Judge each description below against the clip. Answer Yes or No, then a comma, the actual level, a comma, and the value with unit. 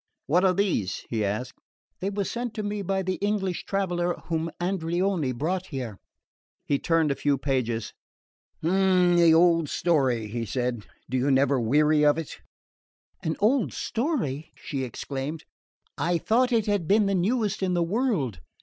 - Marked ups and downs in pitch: Yes, wide, 6.2 semitones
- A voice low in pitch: No, medium, 170 Hz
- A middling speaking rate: Yes, average, 160 wpm